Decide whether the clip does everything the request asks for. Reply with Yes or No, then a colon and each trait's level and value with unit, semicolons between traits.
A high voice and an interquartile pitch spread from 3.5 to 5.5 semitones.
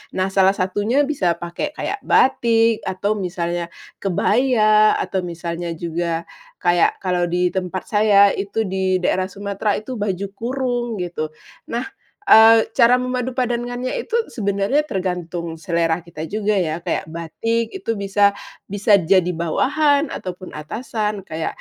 Yes: high, 195 Hz; average, 4.6 semitones